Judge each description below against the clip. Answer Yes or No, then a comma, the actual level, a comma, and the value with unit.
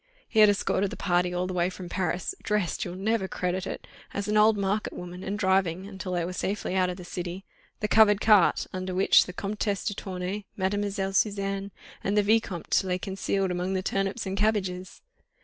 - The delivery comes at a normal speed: Yes, average, 185 wpm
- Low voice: No, high, 190 Hz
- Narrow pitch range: Yes, narrow, 2.0 semitones